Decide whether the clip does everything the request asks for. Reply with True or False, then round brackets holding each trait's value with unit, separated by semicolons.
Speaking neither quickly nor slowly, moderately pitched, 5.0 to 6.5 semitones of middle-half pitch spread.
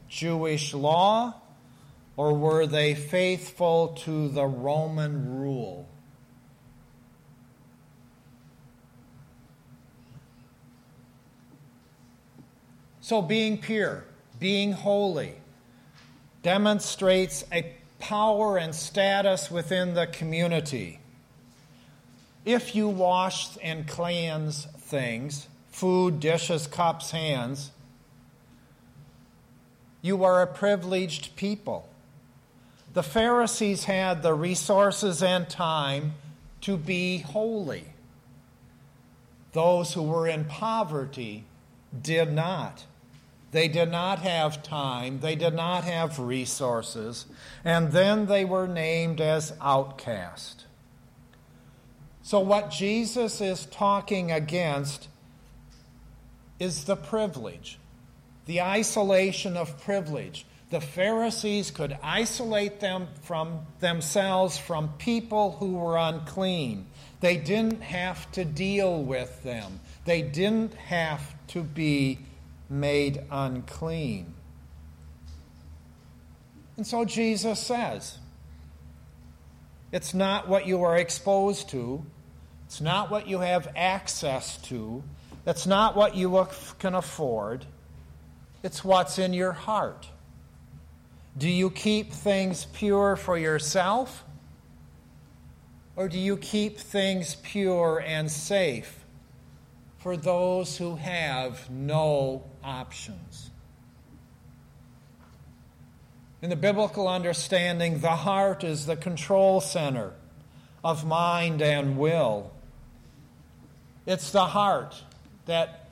False (95 wpm; 165 Hz; 5.3 semitones)